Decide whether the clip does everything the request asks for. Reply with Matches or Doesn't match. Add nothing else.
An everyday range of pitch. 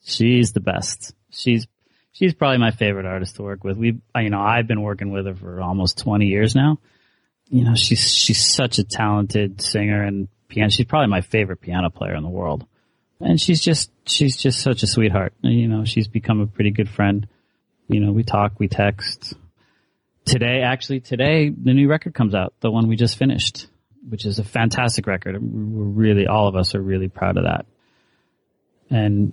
Matches